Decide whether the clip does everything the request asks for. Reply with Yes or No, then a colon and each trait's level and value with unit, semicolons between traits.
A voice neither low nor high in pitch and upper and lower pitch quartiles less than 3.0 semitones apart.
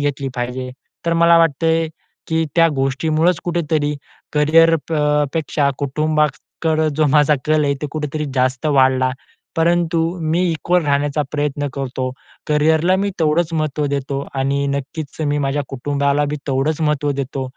Yes: medium, 150 Hz; narrow, 2.4 semitones